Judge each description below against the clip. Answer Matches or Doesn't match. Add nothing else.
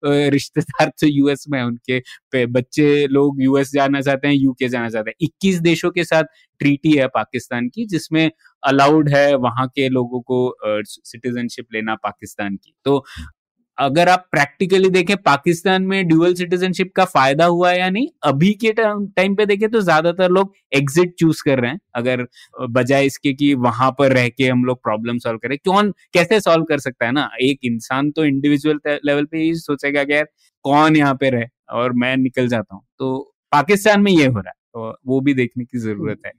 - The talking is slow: Doesn't match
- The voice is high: Doesn't match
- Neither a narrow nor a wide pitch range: Matches